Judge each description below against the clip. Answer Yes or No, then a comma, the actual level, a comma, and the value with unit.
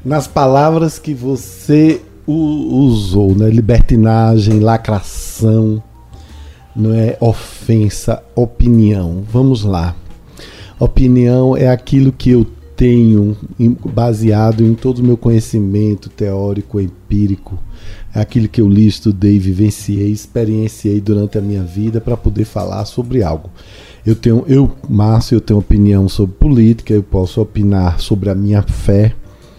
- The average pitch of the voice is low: Yes, low, 110 Hz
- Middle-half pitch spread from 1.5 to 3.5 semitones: Yes, average, 2.7 semitones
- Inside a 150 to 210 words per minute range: No, slow, 120 wpm